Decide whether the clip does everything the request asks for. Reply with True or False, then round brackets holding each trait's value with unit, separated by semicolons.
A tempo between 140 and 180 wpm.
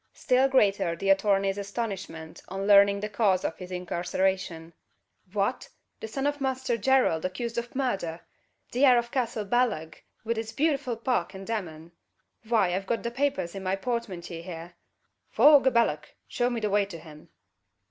True (170 wpm)